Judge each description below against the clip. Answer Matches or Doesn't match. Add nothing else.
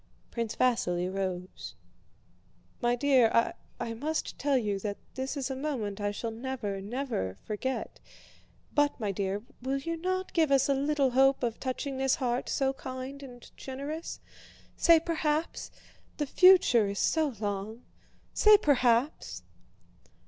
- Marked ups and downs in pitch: Doesn't match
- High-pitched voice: Matches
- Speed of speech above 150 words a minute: Doesn't match